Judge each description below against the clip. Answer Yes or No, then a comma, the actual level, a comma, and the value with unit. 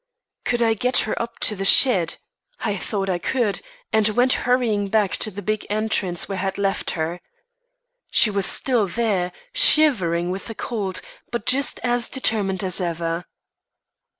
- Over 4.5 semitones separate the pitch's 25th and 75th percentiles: No, average, 3.9 semitones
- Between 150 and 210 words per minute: Yes, average, 170 wpm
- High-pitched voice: Yes, high, 205 Hz